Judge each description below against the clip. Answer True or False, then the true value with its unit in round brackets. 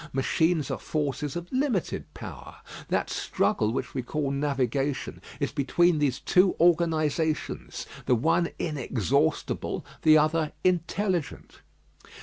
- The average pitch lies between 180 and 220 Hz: False (155 Hz)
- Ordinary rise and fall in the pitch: True (3.7 semitones)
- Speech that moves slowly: True (115 wpm)